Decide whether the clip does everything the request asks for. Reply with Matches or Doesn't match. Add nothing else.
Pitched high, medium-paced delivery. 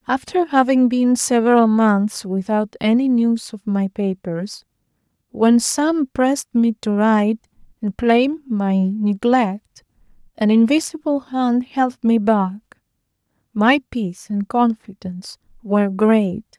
Doesn't match